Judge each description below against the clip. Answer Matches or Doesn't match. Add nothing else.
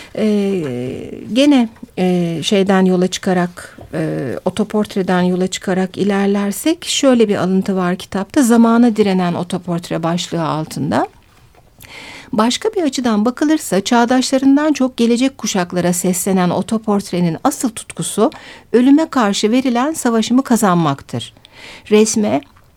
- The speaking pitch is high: Matches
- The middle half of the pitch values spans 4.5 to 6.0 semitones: Matches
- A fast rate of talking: Doesn't match